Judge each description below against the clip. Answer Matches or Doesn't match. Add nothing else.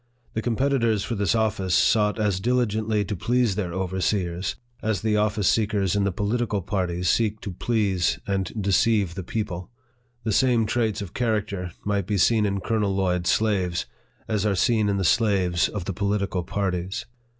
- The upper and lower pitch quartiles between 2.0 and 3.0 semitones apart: Matches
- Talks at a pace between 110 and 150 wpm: Doesn't match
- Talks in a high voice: Doesn't match